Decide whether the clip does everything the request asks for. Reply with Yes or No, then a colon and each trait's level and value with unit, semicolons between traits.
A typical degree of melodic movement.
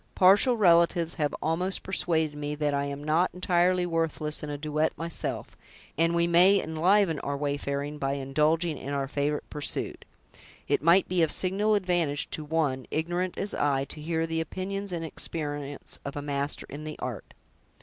Yes: average, 3.1 semitones